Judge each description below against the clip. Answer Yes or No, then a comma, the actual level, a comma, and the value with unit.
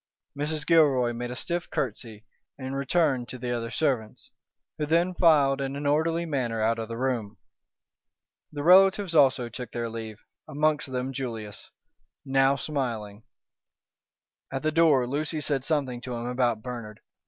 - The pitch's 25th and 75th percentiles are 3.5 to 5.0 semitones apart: Yes, average, 4.1 semitones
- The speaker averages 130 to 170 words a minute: Yes, average, 155 wpm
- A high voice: No, low, 135 Hz